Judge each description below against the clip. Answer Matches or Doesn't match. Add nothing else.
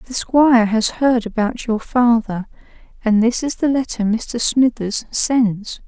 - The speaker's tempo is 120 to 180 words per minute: Matches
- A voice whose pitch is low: Doesn't match